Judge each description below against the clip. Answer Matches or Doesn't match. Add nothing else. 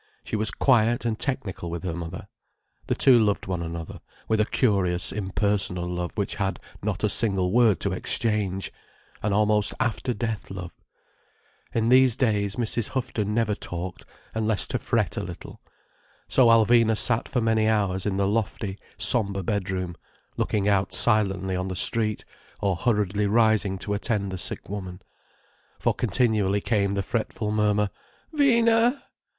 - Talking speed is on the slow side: Doesn't match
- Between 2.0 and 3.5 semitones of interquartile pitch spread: Matches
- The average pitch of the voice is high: Doesn't match